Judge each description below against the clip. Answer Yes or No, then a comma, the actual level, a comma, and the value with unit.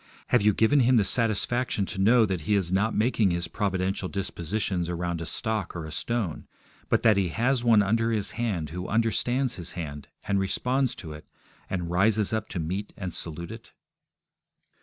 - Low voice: Yes, low, 100 Hz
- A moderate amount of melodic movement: Yes, average, 4.4 semitones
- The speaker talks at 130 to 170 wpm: No, average, 185 wpm